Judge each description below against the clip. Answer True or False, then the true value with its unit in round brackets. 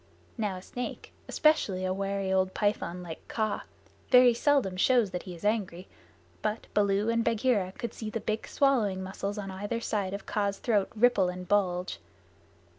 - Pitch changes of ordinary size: True (3.3 semitones)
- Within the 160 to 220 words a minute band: True (170 wpm)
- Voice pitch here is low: False (205 Hz)